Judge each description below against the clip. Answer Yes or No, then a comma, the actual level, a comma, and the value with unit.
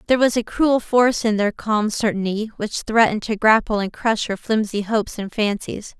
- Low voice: No, high, 215 Hz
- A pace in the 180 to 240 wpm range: Yes, average, 200 wpm